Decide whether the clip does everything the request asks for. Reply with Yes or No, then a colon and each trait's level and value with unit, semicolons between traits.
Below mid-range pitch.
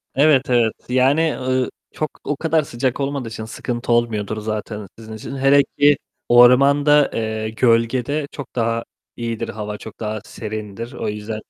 Yes: low, 120 Hz